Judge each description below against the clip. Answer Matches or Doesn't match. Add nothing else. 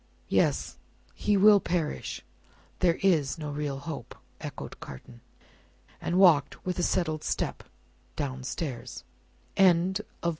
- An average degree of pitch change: Matches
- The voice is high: Doesn't match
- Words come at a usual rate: Doesn't match